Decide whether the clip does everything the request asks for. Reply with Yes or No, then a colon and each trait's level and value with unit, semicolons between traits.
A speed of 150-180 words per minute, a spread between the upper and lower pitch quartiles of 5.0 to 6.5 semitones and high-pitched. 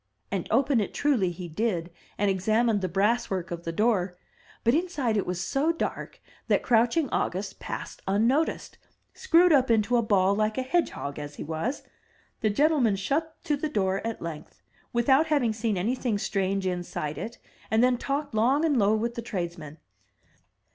Yes: average, 175 wpm; wide, 5.6 semitones; high, 220 Hz